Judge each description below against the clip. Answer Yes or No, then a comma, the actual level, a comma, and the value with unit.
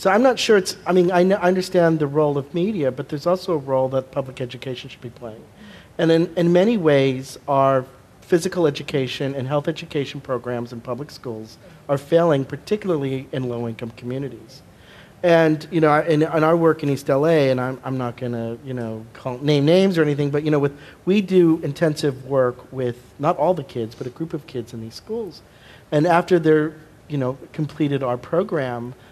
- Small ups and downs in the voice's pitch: No, average, 4.5 semitones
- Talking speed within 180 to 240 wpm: Yes, average, 200 wpm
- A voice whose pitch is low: No, medium, 145 Hz